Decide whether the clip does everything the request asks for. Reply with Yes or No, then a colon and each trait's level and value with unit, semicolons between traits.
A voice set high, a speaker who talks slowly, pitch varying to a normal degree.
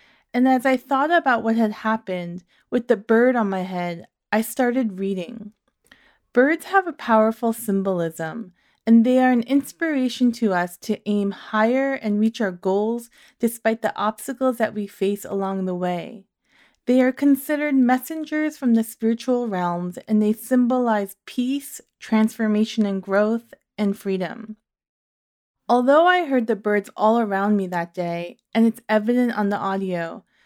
No: high, 220 Hz; average, 155 wpm; average, 4.3 semitones